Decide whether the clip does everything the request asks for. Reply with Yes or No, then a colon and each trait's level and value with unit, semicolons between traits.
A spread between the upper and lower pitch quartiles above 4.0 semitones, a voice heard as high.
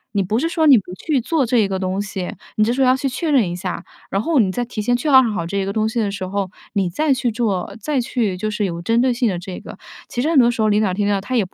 Yes: average, 4.4 semitones; high, 215 Hz